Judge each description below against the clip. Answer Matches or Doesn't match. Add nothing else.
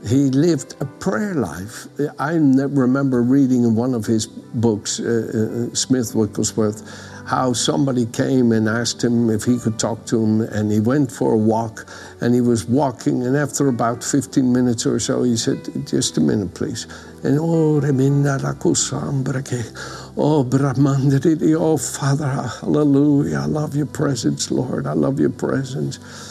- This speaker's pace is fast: Doesn't match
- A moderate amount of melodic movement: Matches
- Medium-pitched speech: Doesn't match